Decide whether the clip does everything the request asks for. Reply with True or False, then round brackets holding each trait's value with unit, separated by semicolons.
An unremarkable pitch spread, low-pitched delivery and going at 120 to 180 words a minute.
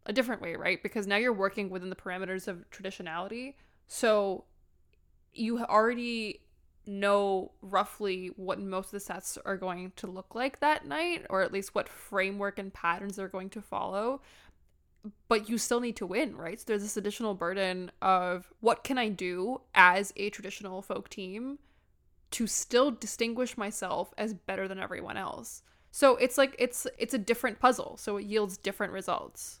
False (3.6 semitones; 200 Hz; 170 wpm)